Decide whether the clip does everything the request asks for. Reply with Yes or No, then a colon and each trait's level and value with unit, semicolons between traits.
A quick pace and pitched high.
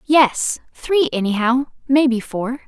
No: slow, 90 wpm; very high, 255 Hz